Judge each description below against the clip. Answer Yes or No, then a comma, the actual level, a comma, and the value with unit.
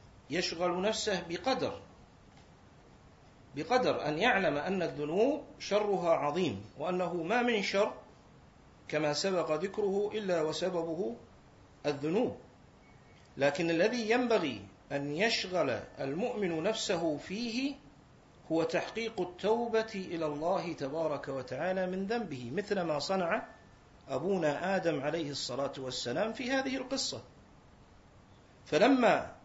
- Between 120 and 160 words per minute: No, average, 100 wpm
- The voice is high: No, medium, 180 Hz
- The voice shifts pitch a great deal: Yes, wide, 6.4 semitones